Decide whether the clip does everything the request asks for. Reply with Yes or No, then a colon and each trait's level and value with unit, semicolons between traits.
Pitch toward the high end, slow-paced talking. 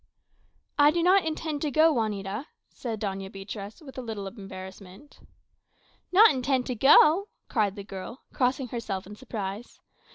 No: high, 230 Hz; average, 150 wpm